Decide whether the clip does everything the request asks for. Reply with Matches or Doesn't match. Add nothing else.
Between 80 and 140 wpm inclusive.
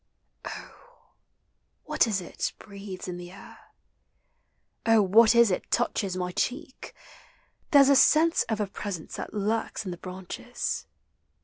Matches